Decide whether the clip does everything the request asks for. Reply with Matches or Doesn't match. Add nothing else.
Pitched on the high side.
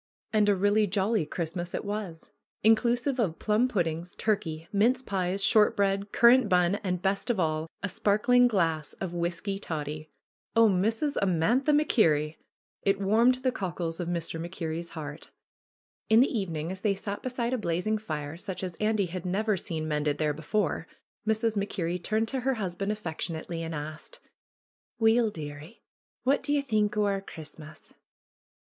Matches